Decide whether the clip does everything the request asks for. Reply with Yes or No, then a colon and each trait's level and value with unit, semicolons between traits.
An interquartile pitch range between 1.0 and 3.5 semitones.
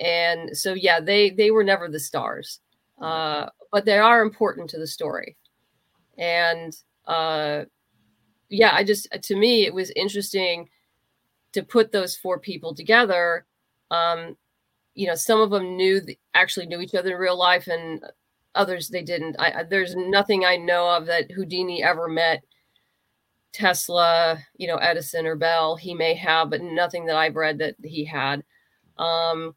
Yes: average, 2.9 semitones